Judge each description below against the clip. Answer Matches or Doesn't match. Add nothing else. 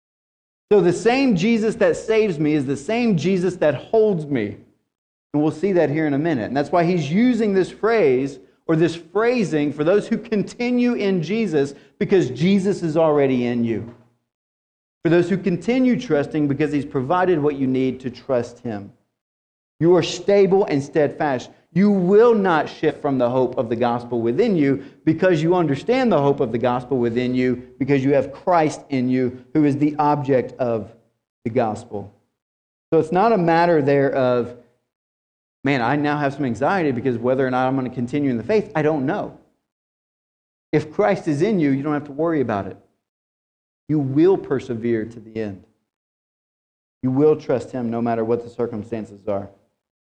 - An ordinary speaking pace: Matches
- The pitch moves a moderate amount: Doesn't match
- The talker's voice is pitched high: Doesn't match